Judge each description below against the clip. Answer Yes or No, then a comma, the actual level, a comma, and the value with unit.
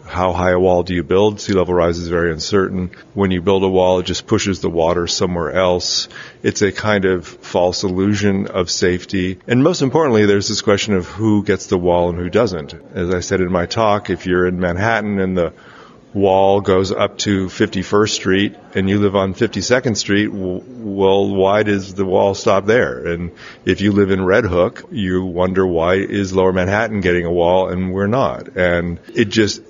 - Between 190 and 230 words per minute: Yes, average, 200 wpm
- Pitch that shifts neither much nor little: No, narrow, 2.0 semitones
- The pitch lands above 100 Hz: No, very low, 95 Hz